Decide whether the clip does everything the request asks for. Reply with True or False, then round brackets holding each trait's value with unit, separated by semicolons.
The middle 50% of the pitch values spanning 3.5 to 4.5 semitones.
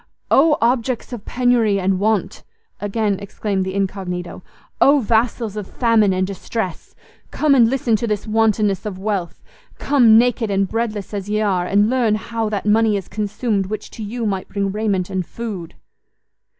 False (2.7 semitones)